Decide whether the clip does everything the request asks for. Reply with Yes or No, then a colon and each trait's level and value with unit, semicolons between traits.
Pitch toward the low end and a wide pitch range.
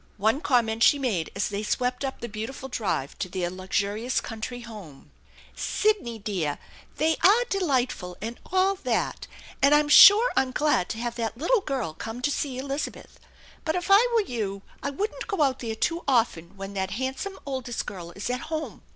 No: high, 245 Hz; wide, 6.2 semitones